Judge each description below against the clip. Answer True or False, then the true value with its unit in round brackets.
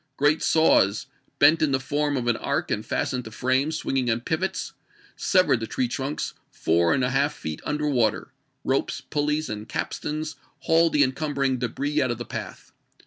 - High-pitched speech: False (135 Hz)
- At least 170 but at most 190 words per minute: True (185 wpm)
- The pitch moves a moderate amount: True (3.7 semitones)